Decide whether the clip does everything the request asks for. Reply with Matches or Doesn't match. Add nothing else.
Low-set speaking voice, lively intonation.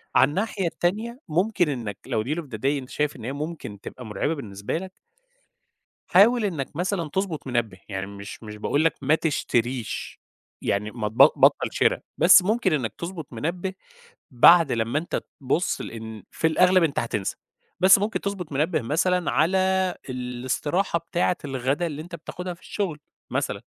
Doesn't match